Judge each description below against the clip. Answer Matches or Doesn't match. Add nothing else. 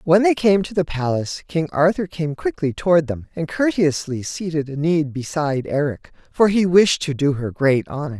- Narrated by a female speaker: Matches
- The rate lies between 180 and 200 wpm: Matches